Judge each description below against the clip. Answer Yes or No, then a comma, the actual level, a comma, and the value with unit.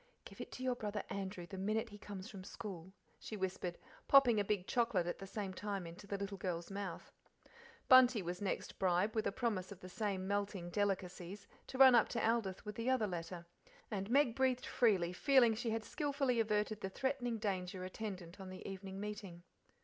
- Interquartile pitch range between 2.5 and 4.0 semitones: Yes, average, 3.4 semitones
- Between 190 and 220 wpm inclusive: Yes, average, 200 wpm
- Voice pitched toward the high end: Yes, high, 200 Hz